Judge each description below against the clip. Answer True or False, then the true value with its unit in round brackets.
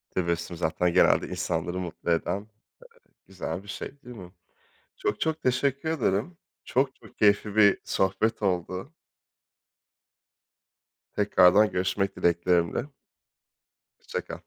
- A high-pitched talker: False (100 Hz)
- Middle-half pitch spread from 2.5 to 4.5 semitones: True (3.9 semitones)